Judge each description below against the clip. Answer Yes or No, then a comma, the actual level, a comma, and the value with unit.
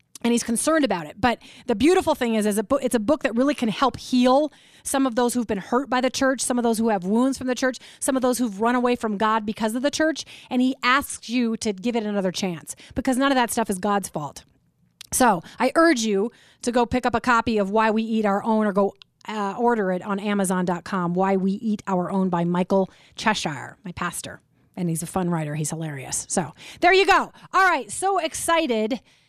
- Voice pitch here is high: Yes, high, 225 Hz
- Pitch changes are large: No, average, 4.8 semitones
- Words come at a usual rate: No, fast, 240 wpm